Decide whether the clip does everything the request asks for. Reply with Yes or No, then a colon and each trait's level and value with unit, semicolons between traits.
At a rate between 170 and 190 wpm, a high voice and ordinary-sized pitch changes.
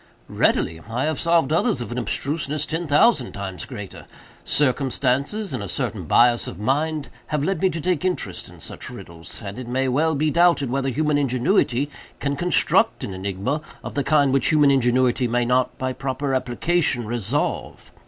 No: average, 175 wpm; low, 135 Hz; average, 4.0 semitones